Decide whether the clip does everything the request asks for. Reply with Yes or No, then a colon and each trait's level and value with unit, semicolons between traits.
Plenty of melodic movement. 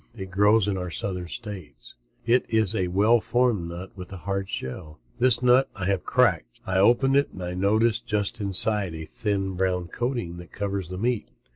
No: average, 3.5 semitones